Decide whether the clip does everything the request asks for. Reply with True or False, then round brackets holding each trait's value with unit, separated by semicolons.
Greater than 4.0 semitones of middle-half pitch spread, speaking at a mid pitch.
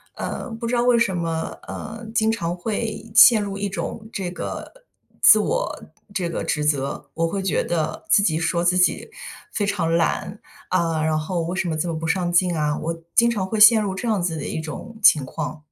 True (4.7 semitones; 180 Hz)